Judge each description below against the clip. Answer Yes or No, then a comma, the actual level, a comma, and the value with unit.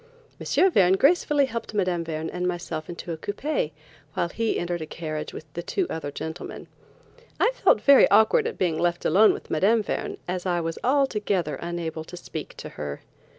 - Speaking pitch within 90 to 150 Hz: No, medium, 180 Hz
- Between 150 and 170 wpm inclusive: No, average, 185 wpm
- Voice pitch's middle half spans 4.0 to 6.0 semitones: Yes, average, 5.2 semitones